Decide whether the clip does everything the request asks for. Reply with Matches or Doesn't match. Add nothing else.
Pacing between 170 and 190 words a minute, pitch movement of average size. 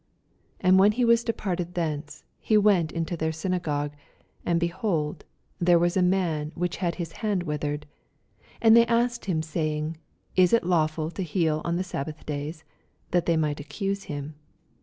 Matches